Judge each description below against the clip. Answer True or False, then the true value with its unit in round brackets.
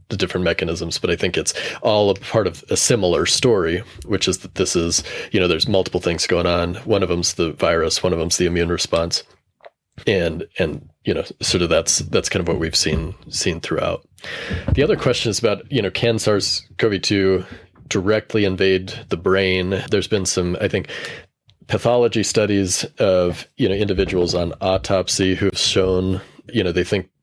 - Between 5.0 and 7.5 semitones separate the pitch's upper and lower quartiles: False (2.6 semitones)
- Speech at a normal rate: True (185 wpm)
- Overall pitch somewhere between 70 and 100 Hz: True (95 Hz)